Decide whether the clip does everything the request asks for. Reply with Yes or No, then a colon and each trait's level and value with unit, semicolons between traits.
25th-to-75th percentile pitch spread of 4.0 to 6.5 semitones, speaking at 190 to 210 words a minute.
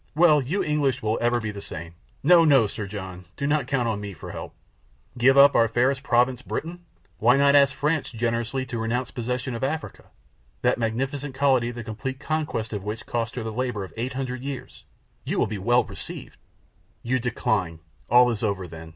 No: average, 3.6 semitones; average, 195 wpm